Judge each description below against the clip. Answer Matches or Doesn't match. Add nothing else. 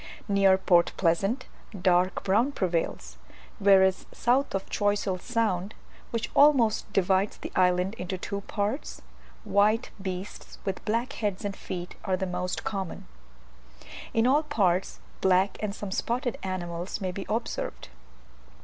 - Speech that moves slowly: Matches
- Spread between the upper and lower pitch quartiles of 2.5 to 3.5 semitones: Matches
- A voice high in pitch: Matches